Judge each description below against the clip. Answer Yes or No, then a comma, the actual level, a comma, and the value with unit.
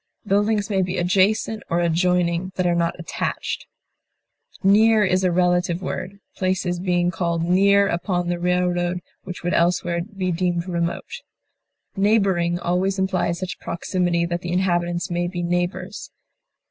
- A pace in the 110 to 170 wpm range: Yes, average, 140 wpm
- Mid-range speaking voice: Yes, medium, 180 Hz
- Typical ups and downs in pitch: No, narrow, 1.6 semitones